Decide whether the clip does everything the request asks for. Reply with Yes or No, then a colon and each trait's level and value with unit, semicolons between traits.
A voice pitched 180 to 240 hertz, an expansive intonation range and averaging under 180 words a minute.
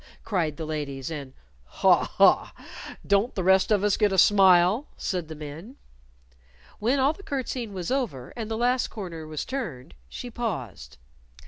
Yes: high, 190 Hz; wide, 7.0 semitones; average, 160 wpm